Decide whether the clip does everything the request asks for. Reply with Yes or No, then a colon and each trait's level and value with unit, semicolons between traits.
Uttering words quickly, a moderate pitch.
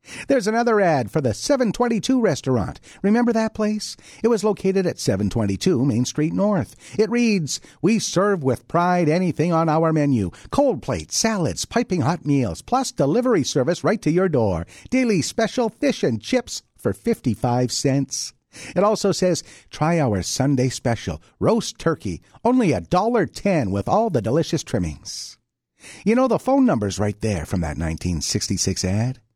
No: average, 160 wpm; medium, 160 Hz